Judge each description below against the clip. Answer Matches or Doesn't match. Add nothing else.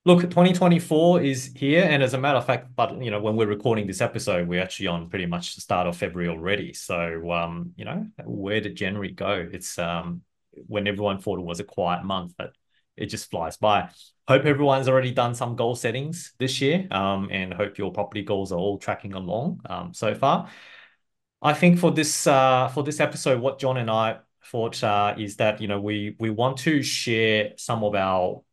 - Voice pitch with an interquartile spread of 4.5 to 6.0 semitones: Matches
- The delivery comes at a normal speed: Doesn't match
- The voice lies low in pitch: Matches